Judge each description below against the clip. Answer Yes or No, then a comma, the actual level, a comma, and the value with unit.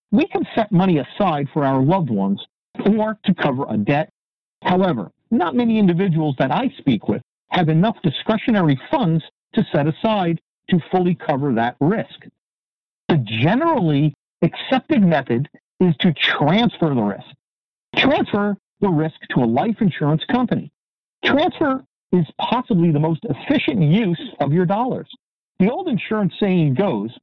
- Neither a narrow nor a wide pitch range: No, wide, 6.0 semitones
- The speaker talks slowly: No, average, 145 wpm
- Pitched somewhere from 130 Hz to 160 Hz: No, medium, 180 Hz